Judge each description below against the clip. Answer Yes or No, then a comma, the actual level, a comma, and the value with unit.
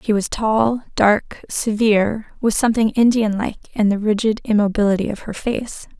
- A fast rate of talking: No, average, 160 wpm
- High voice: Yes, high, 215 Hz